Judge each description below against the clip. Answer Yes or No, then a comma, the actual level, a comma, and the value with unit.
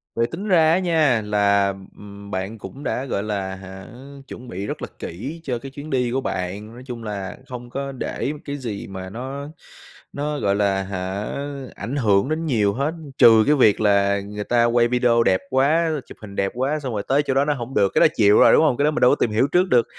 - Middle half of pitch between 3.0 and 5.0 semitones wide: No, wide, 5.4 semitones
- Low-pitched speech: Yes, low, 120 Hz